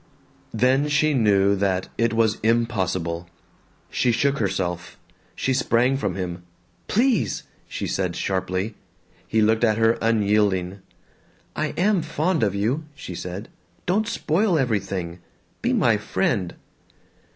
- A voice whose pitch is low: Yes, low, 110 Hz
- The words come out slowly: Yes, slow, 125 wpm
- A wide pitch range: Yes, wide, 6.1 semitones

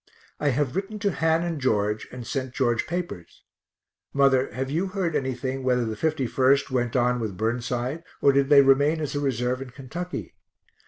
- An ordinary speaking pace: Yes, average, 175 wpm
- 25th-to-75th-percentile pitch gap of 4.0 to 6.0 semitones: No, average, 3.6 semitones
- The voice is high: No, low, 135 Hz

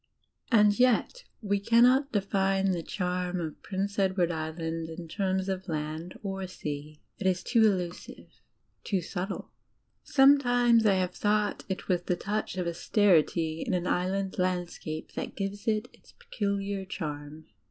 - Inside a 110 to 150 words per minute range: Yes, average, 145 wpm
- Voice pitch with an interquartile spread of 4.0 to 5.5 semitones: No, average, 2.9 semitones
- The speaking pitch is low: No, high, 190 Hz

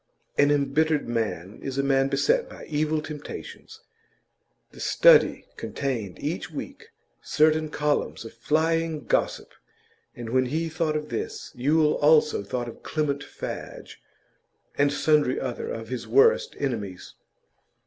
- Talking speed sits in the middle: No, slow, 130 wpm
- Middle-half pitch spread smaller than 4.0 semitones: Yes, average, 3.6 semitones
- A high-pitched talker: No, medium, 145 Hz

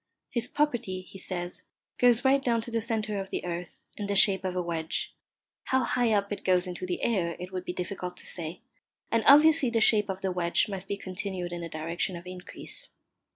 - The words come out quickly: Yes, fast, 215 wpm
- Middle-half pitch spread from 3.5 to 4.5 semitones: Yes, average, 4.2 semitones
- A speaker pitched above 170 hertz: Yes, high, 190 Hz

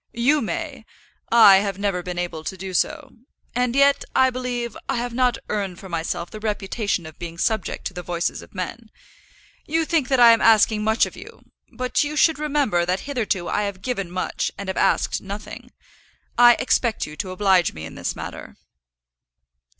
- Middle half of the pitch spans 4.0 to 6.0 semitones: Yes, average, 5.2 semitones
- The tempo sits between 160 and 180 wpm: No, average, 190 wpm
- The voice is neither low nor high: No, high, 215 Hz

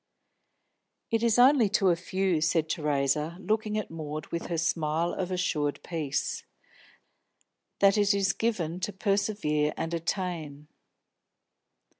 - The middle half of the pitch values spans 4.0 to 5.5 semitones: Yes, average, 4.4 semitones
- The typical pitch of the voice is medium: Yes, medium, 175 Hz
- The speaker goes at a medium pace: No, slow, 120 wpm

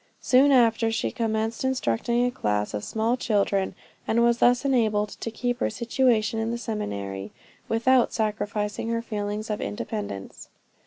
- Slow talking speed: No, average, 150 wpm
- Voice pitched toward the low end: No, high, 225 Hz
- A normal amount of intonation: No, narrow, 2.3 semitones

